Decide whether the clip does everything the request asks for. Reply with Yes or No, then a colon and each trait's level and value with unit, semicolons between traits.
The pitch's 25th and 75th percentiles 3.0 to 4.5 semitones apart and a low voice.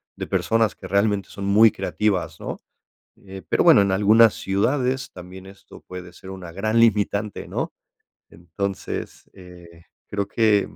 No: narrow, 2.5 semitones; low, 100 Hz